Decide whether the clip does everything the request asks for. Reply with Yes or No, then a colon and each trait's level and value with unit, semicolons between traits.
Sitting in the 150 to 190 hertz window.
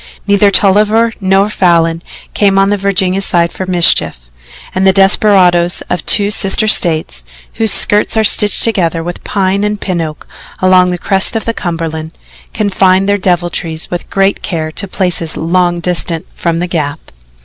Yes: medium, 185 Hz